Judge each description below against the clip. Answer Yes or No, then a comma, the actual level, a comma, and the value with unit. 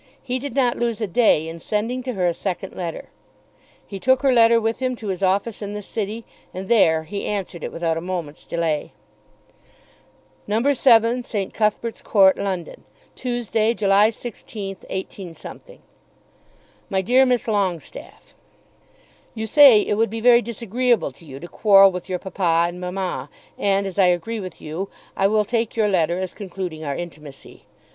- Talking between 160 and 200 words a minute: Yes, average, 165 wpm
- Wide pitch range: No, average, 4.2 semitones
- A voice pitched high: Yes, high, 200 Hz